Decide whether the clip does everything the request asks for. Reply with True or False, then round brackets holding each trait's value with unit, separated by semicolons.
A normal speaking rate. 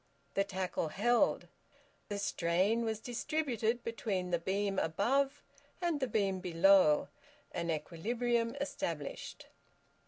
False (105 wpm)